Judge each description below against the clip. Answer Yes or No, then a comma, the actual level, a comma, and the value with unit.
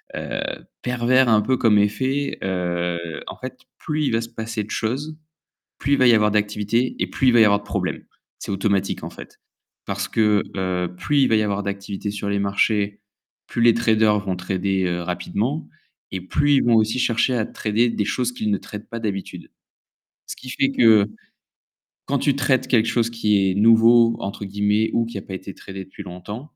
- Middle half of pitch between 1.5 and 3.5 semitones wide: Yes, average, 3.1 semitones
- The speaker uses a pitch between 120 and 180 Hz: No, low, 105 Hz